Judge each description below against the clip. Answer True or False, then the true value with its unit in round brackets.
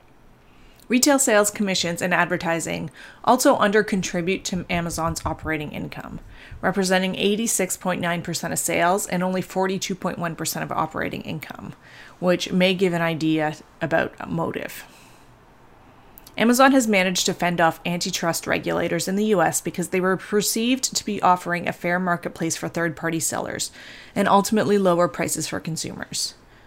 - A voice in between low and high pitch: True (180 Hz)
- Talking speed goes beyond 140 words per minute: False (135 wpm)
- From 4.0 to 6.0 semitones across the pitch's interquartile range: False (2.8 semitones)